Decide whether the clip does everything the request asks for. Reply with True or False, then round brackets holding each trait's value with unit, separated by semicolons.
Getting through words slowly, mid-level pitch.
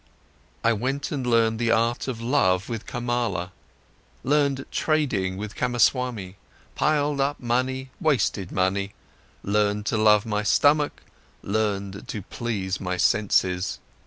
False (125 wpm; 115 Hz)